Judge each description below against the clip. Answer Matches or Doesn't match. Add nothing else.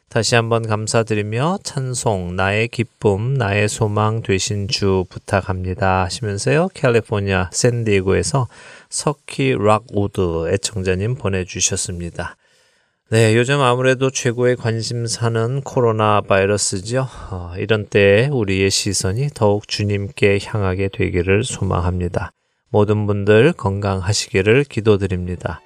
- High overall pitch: Doesn't match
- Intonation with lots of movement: Doesn't match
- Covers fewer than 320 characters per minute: Matches